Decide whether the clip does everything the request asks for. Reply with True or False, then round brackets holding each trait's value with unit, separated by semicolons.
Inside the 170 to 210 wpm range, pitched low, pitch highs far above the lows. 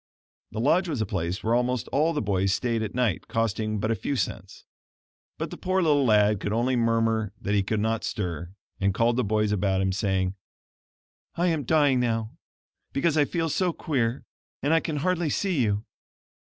True (190 wpm; 115 Hz; 5.7 semitones)